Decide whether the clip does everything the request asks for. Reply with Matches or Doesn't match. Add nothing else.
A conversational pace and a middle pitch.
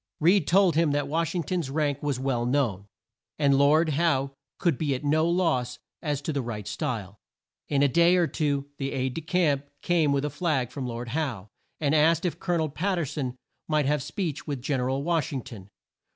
Doesn't match